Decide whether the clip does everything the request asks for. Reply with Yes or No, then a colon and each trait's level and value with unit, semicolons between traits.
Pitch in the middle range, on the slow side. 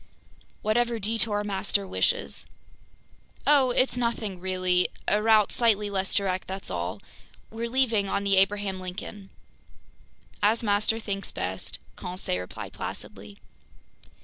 No: high, 200 Hz; slow, 120 wpm